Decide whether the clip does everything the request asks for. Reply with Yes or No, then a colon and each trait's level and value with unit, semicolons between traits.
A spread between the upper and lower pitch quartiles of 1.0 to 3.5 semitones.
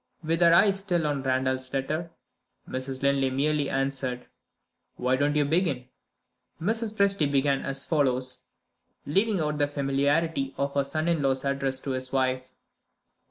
Yes: average, 3.2 semitones